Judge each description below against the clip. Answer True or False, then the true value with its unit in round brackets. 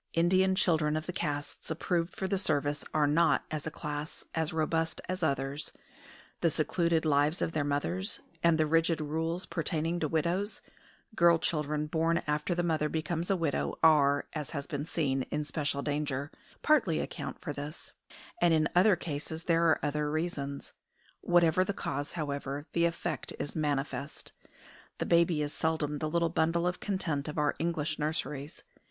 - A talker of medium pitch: True (155 Hz)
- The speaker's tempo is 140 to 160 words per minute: False (170 wpm)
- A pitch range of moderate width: False (2.3 semitones)